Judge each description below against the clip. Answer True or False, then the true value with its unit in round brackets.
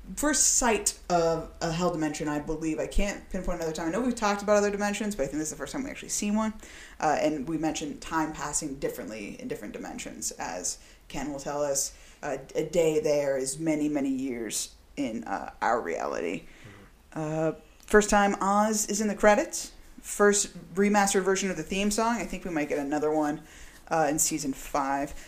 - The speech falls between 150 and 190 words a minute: False (200 wpm)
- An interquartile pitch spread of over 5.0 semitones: True (5.4 semitones)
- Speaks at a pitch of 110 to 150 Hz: False (170 Hz)